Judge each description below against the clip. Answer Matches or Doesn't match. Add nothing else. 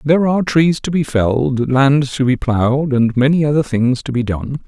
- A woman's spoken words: Doesn't match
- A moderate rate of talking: Doesn't match